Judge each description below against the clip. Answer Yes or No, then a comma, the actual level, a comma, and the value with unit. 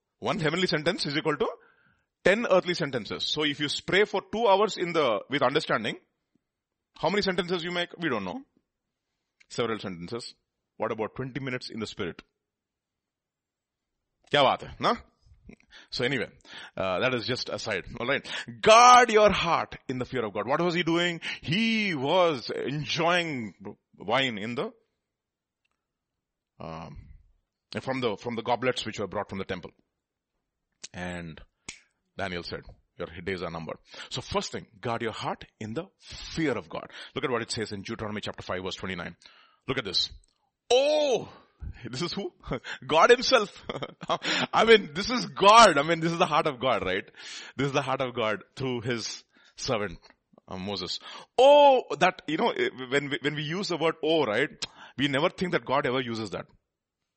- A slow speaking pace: No, average, 165 wpm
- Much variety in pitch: Yes, wide, 9.0 semitones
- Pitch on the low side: No, medium, 145 Hz